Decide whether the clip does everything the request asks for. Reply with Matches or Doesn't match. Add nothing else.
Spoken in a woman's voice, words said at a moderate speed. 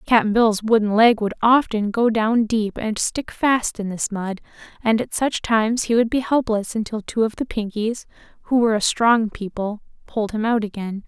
Matches